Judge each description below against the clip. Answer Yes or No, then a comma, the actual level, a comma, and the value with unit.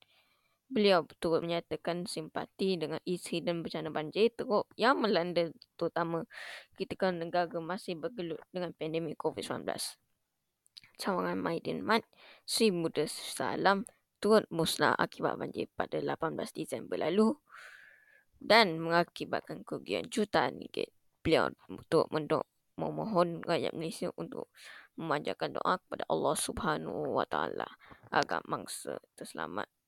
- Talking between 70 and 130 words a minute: Yes, average, 110 wpm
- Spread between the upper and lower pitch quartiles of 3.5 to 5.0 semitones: Yes, average, 4.3 semitones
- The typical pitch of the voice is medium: Yes, medium, 175 Hz